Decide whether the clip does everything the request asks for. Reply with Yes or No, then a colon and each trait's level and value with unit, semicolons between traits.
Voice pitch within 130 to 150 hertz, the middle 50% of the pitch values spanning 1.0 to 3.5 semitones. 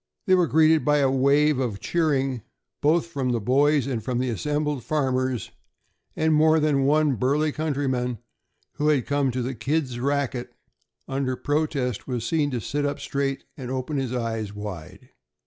Yes: low, 135 Hz; average, 2.9 semitones